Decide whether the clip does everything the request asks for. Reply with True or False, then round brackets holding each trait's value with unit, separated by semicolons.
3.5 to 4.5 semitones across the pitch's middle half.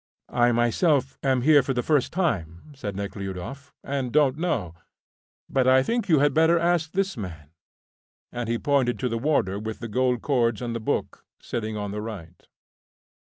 False (5.1 semitones)